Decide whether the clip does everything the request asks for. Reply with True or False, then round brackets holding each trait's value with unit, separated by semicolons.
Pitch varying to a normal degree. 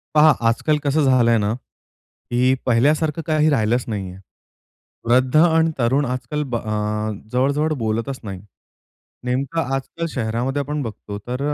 True (4.5 semitones)